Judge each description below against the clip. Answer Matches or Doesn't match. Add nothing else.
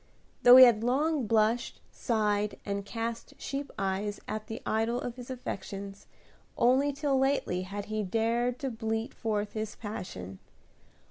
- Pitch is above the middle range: Matches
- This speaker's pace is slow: Doesn't match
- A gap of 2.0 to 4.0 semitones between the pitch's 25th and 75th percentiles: Matches